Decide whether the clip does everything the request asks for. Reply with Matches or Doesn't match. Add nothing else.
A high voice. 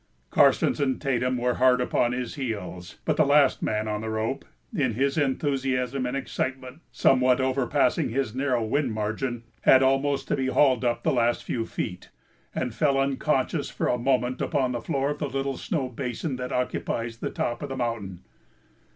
Doesn't match